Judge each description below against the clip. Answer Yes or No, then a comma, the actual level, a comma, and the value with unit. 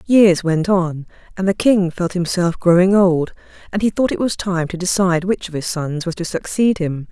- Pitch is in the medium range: Yes, medium, 180 Hz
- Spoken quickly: Yes, fast, 220 wpm